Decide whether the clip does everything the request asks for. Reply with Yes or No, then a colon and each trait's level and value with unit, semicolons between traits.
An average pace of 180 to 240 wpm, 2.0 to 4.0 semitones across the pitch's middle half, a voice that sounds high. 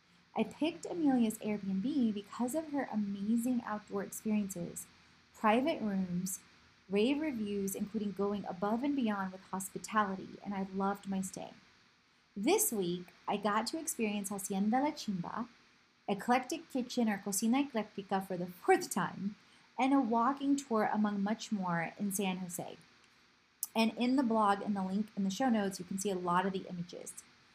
No: average, 160 wpm; average, 3.7 semitones; high, 210 Hz